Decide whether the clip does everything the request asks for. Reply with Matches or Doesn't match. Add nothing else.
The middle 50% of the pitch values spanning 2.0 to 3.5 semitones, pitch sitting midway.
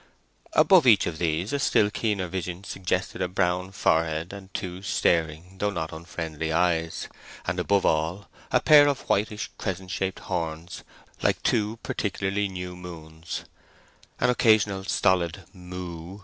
Doesn't match